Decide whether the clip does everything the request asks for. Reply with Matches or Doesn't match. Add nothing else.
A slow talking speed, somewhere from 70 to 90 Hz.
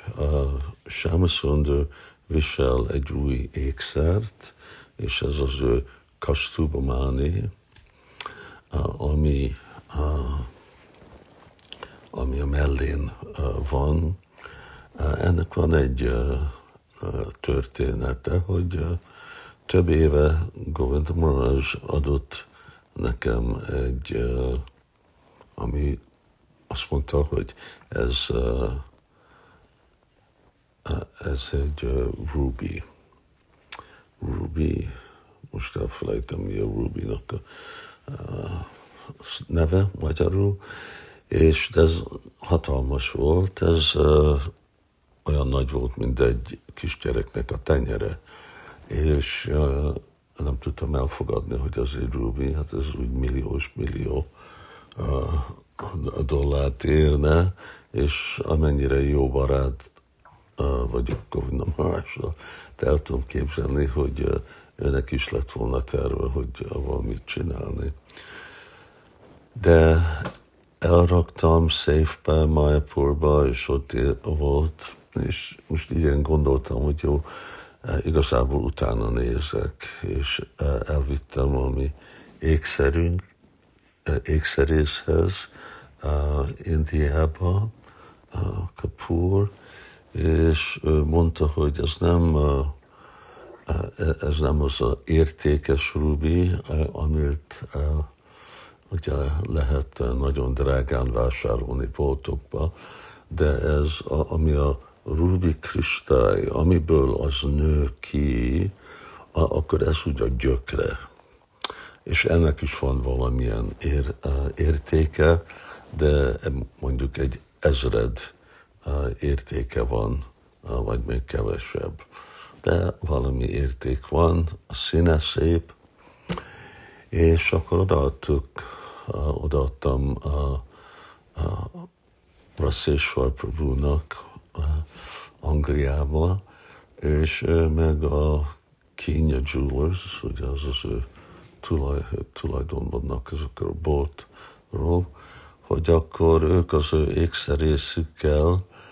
Matches